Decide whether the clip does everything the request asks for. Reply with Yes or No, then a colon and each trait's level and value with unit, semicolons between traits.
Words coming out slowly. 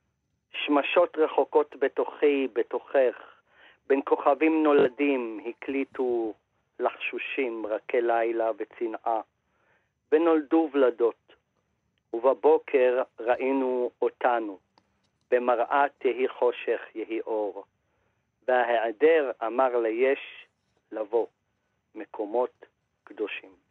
Yes: slow, 75 wpm